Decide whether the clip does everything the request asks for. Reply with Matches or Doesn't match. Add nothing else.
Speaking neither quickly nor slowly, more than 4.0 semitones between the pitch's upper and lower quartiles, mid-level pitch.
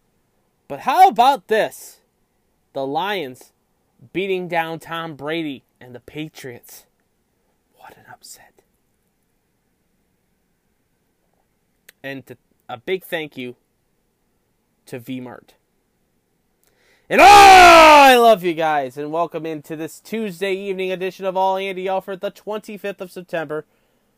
Doesn't match